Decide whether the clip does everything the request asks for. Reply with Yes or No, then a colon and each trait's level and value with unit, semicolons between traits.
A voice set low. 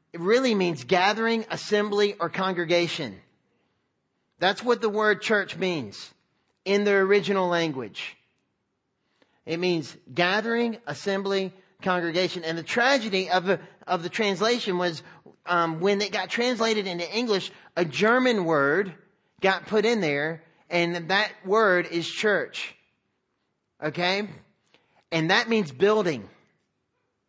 No: high, 190 Hz